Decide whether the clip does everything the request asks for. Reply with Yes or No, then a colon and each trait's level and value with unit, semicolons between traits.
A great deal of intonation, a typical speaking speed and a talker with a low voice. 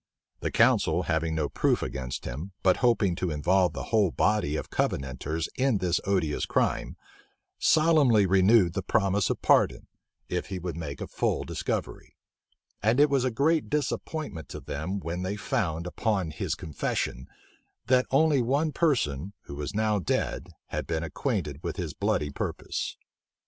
Yes: wide, 6.4 semitones; average, 160 wpm; very low, 95 Hz